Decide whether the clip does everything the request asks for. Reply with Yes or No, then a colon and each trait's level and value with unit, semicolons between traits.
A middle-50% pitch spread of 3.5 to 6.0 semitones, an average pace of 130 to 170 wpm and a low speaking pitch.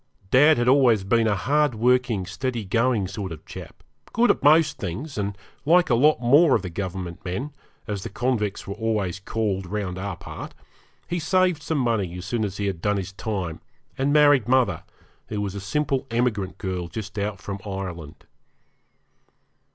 No: average, 5.2 semitones; average, 180 wpm; low, 110 Hz